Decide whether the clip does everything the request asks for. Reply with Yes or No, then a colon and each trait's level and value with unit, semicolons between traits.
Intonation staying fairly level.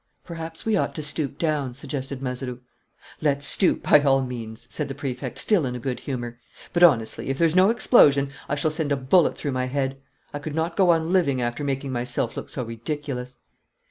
No: average, 3.8 semitones